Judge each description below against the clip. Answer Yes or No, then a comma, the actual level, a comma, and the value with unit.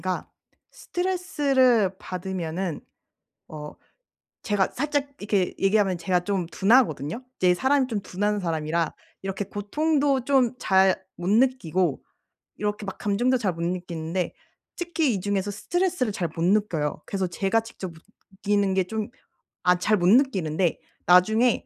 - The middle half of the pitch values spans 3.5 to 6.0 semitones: Yes, average, 5.2 semitones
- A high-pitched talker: Yes, high, 200 Hz